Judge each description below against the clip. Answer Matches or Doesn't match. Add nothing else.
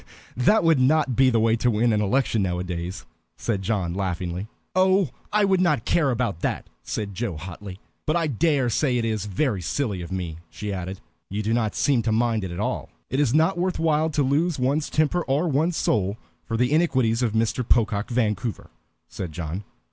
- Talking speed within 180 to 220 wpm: Matches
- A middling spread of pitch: Doesn't match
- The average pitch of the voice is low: Matches